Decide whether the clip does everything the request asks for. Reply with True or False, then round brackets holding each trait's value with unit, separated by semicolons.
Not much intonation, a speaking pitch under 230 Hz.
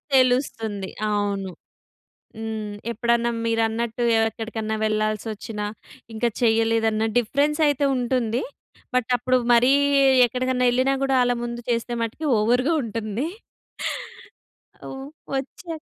False (2.3 semitones; 235 Hz)